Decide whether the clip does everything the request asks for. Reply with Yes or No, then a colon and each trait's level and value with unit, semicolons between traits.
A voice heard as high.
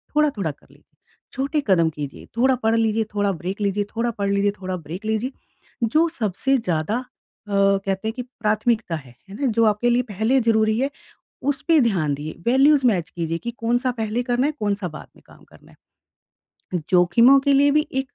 Yes: high, 220 Hz